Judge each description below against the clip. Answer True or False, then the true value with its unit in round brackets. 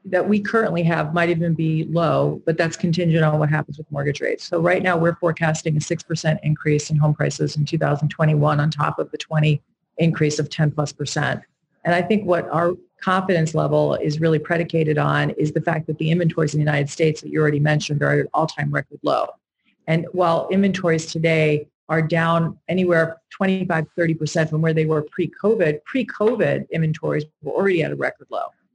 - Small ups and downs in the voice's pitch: True (2.0 semitones)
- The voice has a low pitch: False (160 Hz)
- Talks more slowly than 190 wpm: False (195 wpm)